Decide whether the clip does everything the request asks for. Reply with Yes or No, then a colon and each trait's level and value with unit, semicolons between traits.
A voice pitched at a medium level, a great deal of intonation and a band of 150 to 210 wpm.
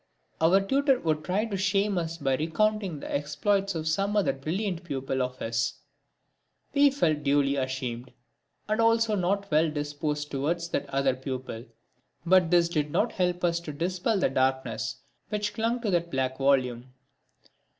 Yes: medium, 165 Hz; wide, 6.4 semitones; average, 155 wpm